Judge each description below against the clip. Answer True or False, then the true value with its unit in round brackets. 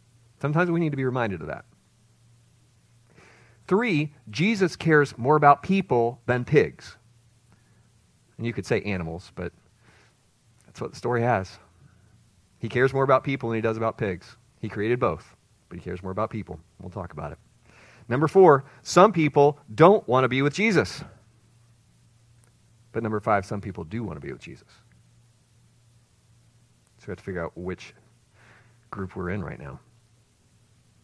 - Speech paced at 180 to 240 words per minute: False (160 wpm)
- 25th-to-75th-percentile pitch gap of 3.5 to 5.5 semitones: False (2.5 semitones)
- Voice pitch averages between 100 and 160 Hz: True (115 Hz)